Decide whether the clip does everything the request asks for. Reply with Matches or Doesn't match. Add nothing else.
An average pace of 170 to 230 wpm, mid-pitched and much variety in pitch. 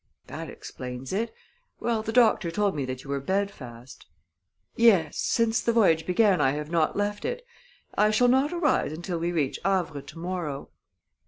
Matches